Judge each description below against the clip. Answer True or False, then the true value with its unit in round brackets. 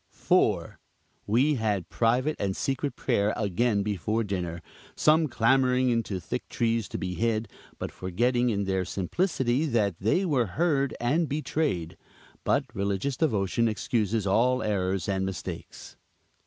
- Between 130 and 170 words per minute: True (135 wpm)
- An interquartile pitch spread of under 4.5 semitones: False (4.8 semitones)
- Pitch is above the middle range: False (115 Hz)